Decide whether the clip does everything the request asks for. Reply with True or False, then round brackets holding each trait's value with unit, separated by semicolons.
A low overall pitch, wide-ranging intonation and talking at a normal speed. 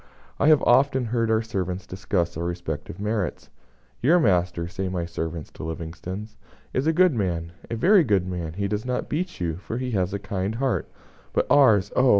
True (100 Hz; 6.0 semitones; 190 wpm)